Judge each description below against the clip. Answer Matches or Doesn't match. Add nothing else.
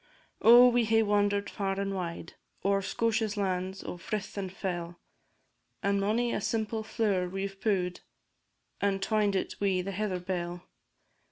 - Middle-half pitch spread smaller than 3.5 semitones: Matches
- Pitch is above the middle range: Matches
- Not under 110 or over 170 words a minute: Matches